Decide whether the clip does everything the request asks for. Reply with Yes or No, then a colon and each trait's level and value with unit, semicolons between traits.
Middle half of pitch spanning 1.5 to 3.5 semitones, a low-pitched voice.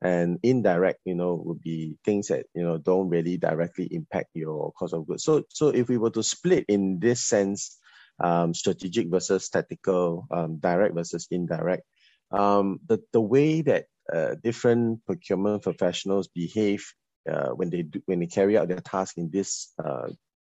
Yes: average, 2.9 semitones; very low, 95 Hz